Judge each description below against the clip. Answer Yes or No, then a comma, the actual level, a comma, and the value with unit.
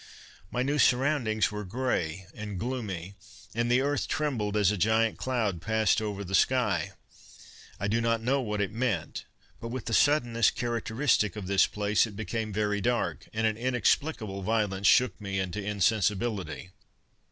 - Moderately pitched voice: No, low, 110 Hz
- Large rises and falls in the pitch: No, average, 3.3 semitones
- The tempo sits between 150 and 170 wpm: Yes, average, 160 wpm